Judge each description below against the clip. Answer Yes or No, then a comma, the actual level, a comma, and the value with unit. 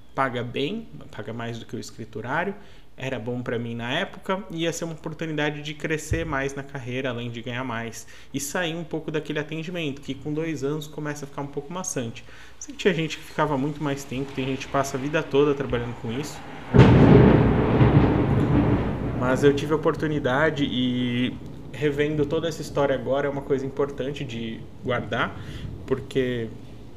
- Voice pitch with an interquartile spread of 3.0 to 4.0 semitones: Yes, average, 3.3 semitones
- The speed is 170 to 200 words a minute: Yes, average, 180 wpm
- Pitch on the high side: No, medium, 140 Hz